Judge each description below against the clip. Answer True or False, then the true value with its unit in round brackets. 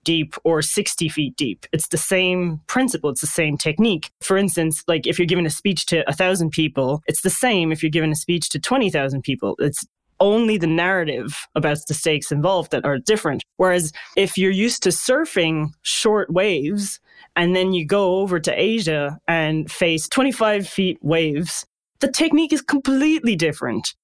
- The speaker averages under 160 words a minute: False (180 wpm)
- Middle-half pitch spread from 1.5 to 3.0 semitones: False (4.1 semitones)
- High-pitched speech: False (175 Hz)